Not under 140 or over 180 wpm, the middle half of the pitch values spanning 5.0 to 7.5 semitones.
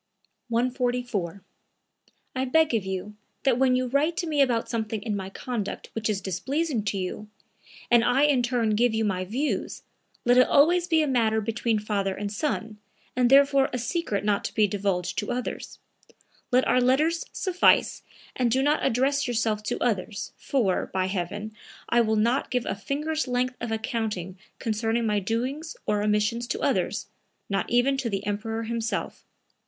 No: average, 170 wpm; average, 3.7 semitones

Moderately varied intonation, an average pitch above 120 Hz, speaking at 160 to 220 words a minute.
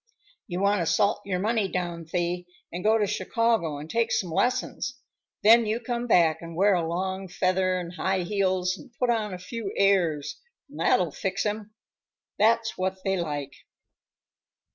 Yes: average, 3.6 semitones; high, 190 Hz; average, 170 wpm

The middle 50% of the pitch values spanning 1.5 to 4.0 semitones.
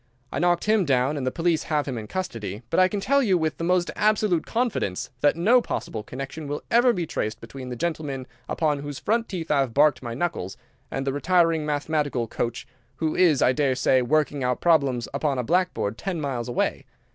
No: average, 5.3 semitones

